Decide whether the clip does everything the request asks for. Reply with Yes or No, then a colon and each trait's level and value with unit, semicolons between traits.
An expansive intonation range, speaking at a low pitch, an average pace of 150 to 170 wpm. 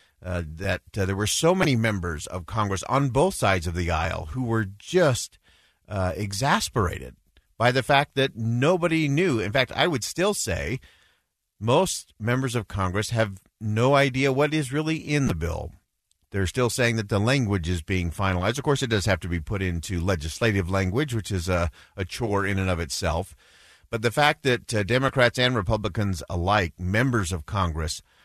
No: wide, 6.1 semitones; low, 105 Hz; average, 185 wpm